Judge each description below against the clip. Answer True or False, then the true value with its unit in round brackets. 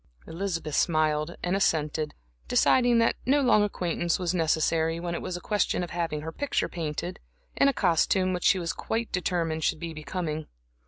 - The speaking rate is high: False (175 wpm)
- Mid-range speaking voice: True (170 Hz)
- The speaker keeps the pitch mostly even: False (3.0 semitones)